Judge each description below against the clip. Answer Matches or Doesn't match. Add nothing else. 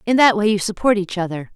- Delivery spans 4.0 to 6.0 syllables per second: Doesn't match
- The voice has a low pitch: Doesn't match